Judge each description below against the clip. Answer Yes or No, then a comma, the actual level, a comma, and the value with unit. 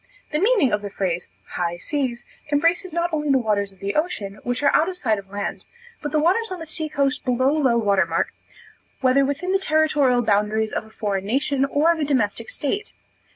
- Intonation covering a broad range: Yes, wide, 6.8 semitones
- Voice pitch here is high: Yes, very high, 270 Hz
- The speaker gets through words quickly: Yes, fast, 210 wpm